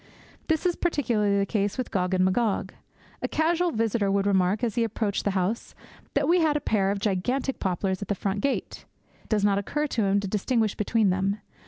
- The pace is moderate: No, fast, 210 wpm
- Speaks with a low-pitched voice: No, high, 205 Hz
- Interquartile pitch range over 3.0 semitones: Yes, average, 4.1 semitones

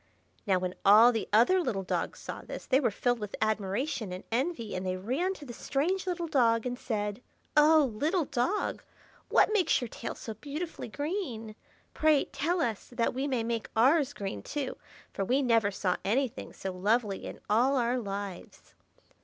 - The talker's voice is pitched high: Yes, high, 240 Hz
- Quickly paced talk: No, average, 180 wpm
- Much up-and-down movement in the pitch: Yes, wide, 5.7 semitones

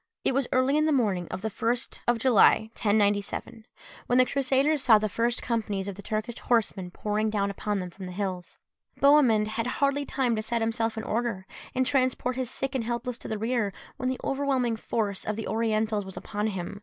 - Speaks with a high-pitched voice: Yes, high, 225 Hz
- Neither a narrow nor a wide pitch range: Yes, average, 3.5 semitones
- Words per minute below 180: No, fast, 205 wpm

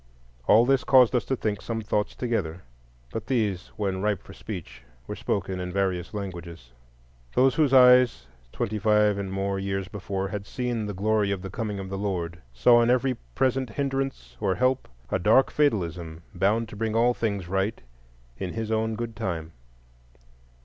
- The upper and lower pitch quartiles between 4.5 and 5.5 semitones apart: No, average, 3.7 semitones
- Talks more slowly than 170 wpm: No, average, 175 wpm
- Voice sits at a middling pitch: No, low, 105 Hz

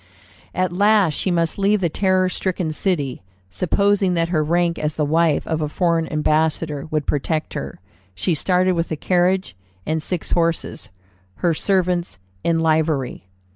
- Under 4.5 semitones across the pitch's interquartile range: Yes, average, 2.8 semitones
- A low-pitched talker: No, medium, 170 Hz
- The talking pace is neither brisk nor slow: Yes, average, 155 wpm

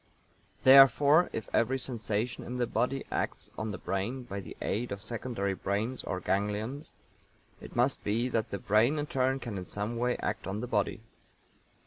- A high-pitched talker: No, low, 115 Hz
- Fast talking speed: No, average, 175 wpm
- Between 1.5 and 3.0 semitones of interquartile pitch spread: No, average, 3.8 semitones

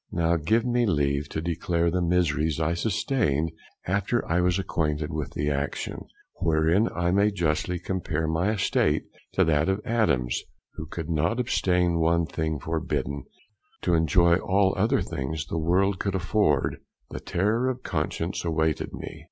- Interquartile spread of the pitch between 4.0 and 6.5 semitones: No, average, 3.3 semitones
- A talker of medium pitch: No, very low, 85 Hz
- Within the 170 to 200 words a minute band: No, average, 155 wpm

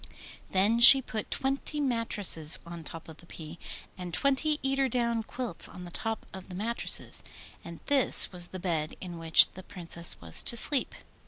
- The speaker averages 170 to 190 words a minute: Yes, average, 175 wpm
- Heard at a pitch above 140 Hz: Yes, high, 190 Hz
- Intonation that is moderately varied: No, wide, 6.4 semitones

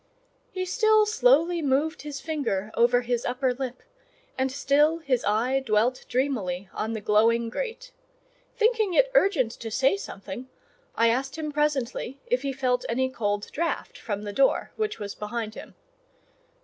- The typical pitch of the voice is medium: No, very high, 260 Hz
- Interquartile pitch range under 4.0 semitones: No, wide, 5.4 semitones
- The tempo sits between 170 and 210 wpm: No, average, 155 wpm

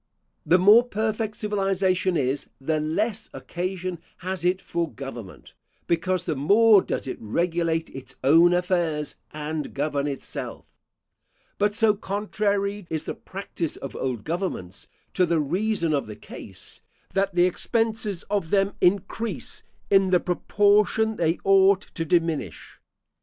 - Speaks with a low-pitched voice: No, medium, 180 Hz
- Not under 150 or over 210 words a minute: No, slow, 135 wpm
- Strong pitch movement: No, average, 4.2 semitones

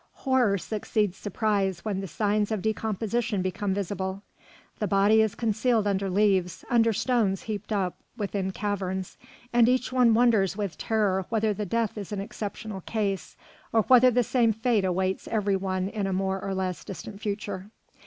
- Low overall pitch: No, high, 205 Hz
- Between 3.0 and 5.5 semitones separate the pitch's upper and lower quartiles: No, narrow, 2.4 semitones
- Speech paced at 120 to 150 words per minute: No, average, 165 wpm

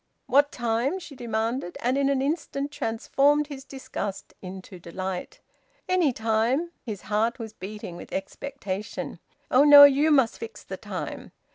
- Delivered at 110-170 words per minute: Yes, average, 145 wpm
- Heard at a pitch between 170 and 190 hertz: No, very high, 255 Hz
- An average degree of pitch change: Yes, average, 4.8 semitones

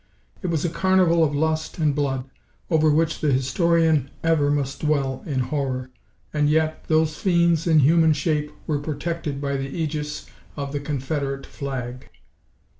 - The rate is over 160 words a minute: No, average, 155 wpm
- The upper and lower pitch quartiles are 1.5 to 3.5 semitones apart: Yes, narrow, 2.5 semitones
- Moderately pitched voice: Yes, medium, 150 Hz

